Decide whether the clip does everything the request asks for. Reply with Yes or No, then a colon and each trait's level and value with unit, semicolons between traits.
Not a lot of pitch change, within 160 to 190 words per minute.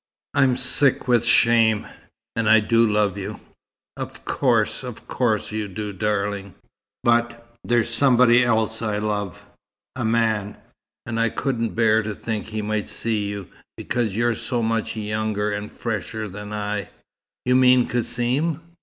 No: narrow, 2.1 semitones; average, 145 wpm